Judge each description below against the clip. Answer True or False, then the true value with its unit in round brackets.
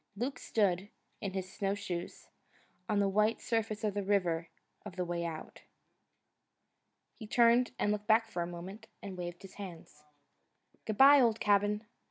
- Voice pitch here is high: True (205 Hz)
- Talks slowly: False (160 wpm)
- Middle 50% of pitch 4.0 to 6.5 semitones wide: False (3.3 semitones)